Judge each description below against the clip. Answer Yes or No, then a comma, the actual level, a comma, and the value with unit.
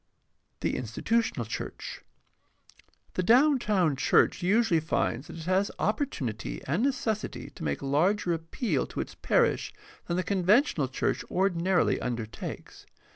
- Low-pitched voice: No, medium, 180 Hz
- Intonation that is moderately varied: No, wide, 7.0 semitones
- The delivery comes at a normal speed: No, slow, 130 wpm